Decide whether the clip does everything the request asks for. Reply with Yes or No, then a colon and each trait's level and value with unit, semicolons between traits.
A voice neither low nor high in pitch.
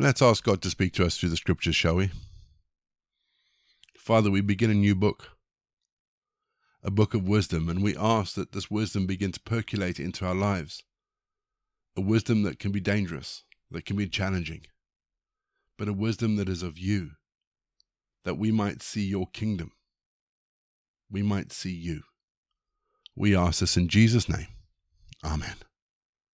No: low, 100 Hz